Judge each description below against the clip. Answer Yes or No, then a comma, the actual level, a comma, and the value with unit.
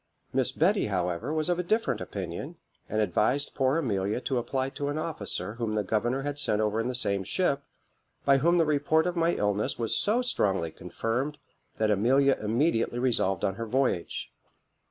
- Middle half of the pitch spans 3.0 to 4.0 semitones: No, wide, 5.6 semitones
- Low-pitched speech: Yes, low, 125 Hz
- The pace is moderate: Yes, average, 180 wpm